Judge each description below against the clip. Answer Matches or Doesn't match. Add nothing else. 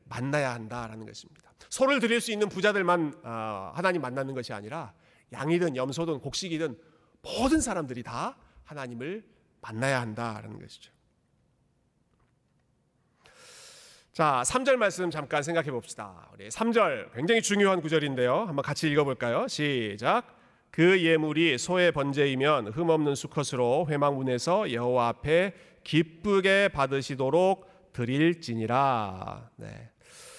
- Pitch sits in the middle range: Matches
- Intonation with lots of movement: Matches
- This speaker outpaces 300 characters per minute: Doesn't match